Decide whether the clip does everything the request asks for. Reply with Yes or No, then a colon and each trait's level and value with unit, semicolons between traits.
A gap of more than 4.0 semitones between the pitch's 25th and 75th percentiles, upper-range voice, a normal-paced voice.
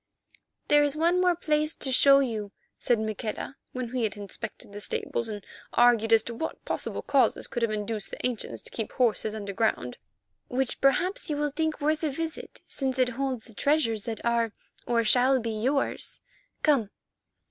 Yes: average, 4.7 semitones; high, 245 Hz; average, 180 wpm